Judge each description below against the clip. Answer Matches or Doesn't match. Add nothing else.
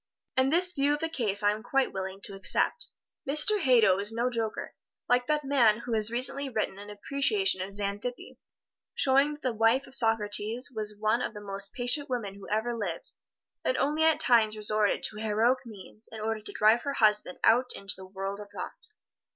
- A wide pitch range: Doesn't match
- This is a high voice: Matches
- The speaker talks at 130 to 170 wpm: Doesn't match